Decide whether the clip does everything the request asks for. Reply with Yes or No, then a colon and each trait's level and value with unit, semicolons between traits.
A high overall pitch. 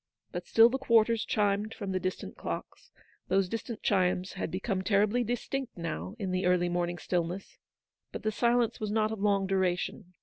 Yes: high, 200 Hz